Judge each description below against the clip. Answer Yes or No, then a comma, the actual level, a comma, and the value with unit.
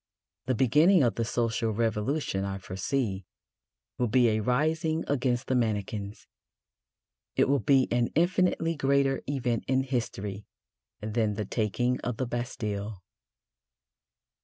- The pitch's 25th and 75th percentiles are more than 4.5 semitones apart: No, average, 4.1 semitones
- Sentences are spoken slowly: Yes, slow, 125 wpm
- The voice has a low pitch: Yes, low, 120 Hz